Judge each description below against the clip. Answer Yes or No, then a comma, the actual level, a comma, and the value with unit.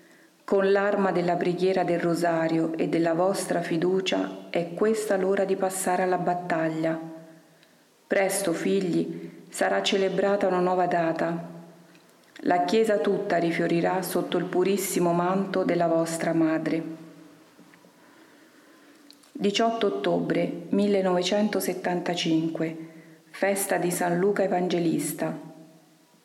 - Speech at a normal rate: No, slow, 100 wpm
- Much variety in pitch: No, average, 3.0 semitones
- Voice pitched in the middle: Yes, medium, 180 Hz